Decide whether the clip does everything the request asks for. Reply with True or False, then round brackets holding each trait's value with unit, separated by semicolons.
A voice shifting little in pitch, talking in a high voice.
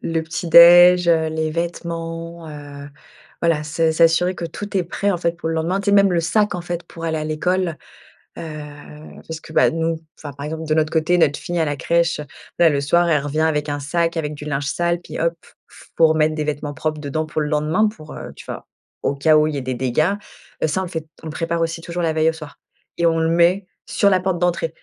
False (2.0 semitones; 165 Hz)